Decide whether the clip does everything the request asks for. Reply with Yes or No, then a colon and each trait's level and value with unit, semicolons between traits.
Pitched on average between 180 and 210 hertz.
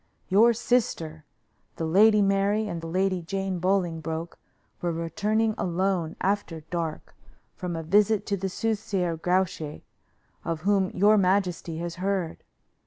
Yes: medium, 185 Hz